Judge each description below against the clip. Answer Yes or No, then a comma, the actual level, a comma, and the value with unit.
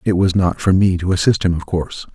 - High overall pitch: No, very low, 90 Hz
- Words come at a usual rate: No, fast, 280 wpm